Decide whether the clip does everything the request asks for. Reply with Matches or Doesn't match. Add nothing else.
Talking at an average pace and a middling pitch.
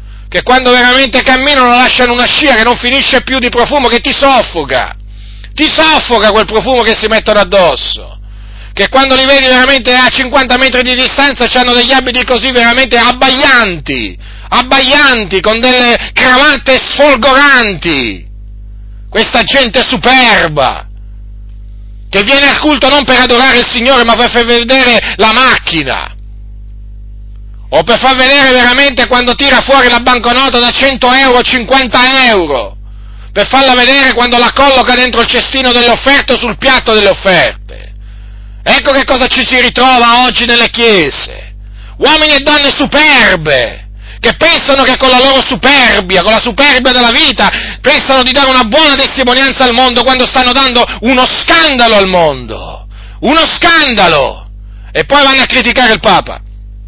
Doesn't match